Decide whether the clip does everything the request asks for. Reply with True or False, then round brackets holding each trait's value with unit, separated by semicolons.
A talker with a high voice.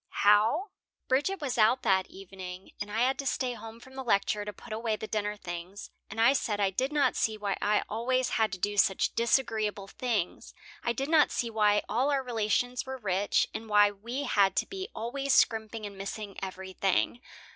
True (220 Hz)